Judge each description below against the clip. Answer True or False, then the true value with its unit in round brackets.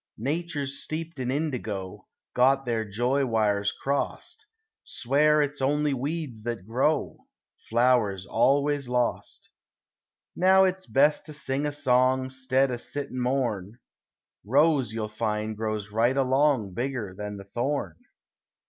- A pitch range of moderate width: True (4.4 semitones)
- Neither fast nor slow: False (130 wpm)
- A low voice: True (130 Hz)